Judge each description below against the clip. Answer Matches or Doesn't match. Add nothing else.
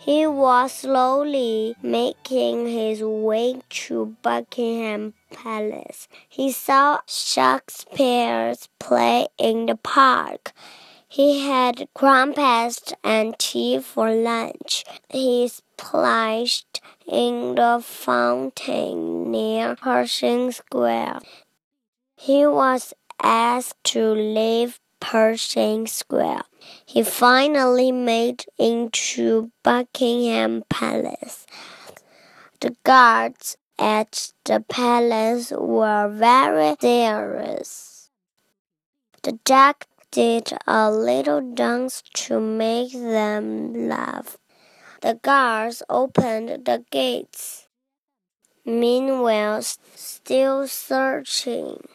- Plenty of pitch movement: Matches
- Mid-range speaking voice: Doesn't match